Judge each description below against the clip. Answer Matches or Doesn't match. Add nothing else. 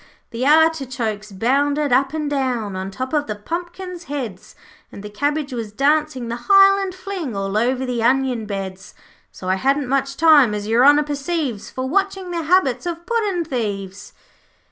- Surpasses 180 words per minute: Doesn't match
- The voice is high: Matches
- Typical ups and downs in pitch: Doesn't match